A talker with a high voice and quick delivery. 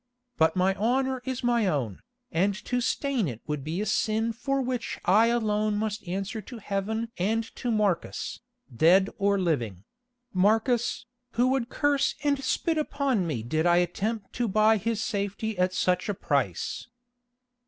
No: high, 215 Hz; average, 155 wpm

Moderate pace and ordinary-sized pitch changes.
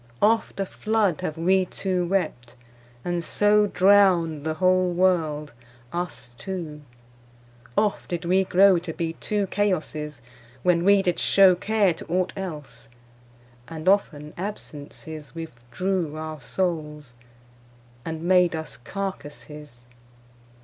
No: slow, 120 wpm; average, 3.7 semitones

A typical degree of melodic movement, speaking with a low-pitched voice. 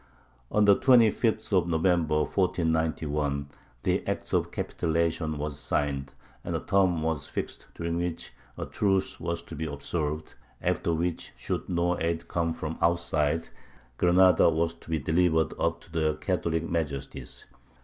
No: narrow, 2.0 semitones; very low, 80 Hz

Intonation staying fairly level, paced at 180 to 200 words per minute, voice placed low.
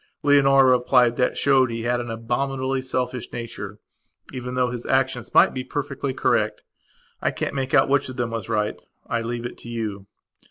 Yes: narrow, 2.2 semitones; average, 185 wpm; low, 125 Hz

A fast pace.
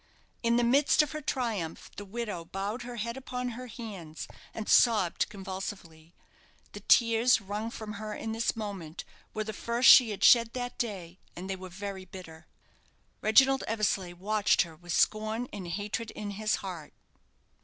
No: average, 165 wpm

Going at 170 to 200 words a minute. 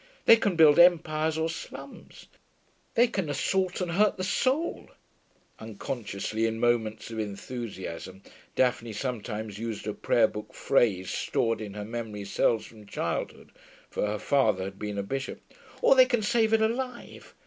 No: average, 155 wpm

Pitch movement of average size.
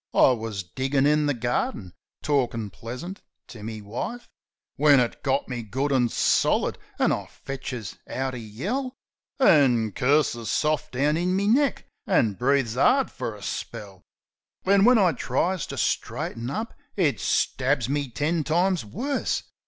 No: wide, 6.5 semitones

